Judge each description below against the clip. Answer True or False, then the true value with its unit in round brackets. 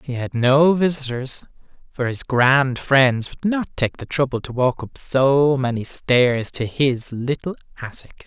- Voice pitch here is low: True (130 Hz)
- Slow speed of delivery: False (165 wpm)